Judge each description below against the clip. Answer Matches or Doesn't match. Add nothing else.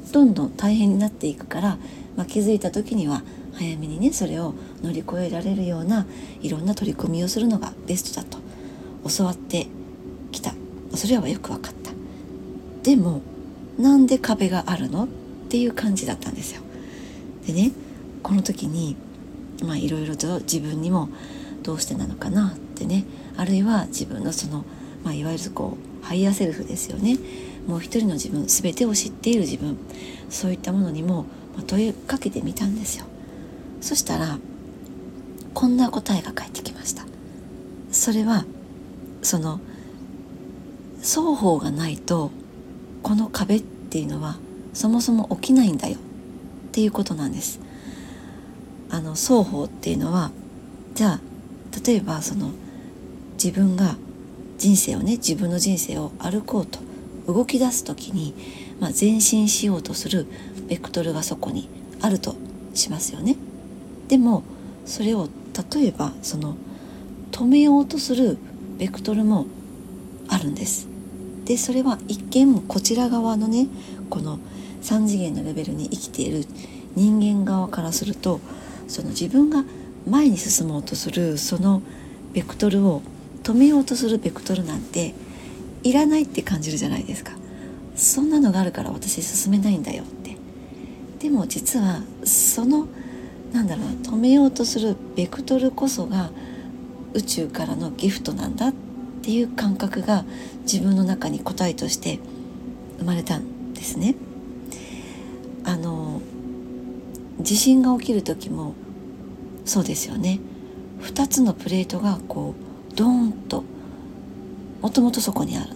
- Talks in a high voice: Matches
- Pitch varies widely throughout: Matches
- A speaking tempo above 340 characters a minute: Doesn't match